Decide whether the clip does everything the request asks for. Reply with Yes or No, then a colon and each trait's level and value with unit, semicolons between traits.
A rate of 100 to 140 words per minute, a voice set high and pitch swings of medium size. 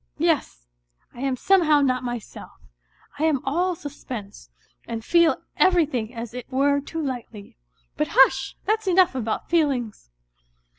Yes: slow, 135 wpm; very high, 270 Hz; average, 5.0 semitones